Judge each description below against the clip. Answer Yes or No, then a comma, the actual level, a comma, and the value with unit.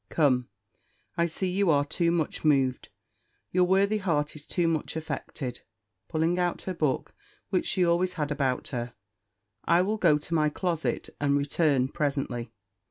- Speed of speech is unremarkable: Yes, average, 160 wpm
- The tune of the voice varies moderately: Yes, average, 3.8 semitones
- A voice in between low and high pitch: Yes, medium, 155 Hz